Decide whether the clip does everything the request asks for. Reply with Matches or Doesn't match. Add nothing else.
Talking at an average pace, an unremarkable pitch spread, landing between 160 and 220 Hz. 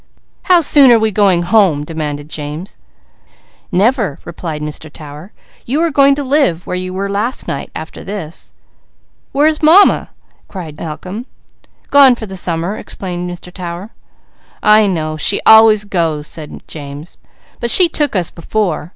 Doesn't match